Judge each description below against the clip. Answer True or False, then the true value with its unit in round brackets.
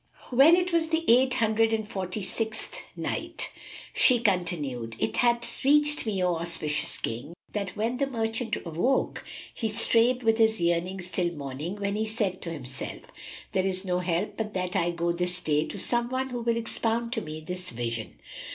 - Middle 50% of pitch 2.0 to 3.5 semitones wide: False (5.3 semitones)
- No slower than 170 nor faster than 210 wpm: True (180 wpm)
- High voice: True (205 Hz)